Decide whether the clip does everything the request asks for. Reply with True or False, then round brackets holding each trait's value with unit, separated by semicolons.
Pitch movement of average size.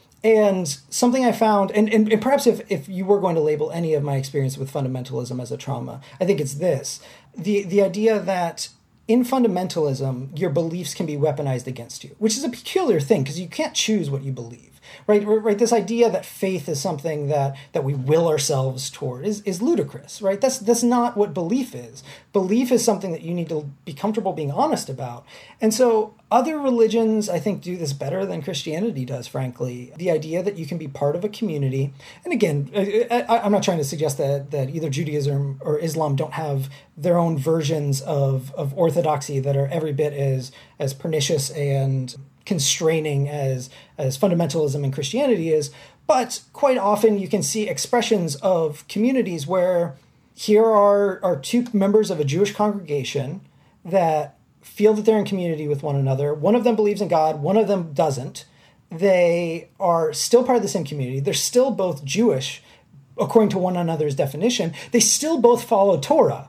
False (6.6 semitones)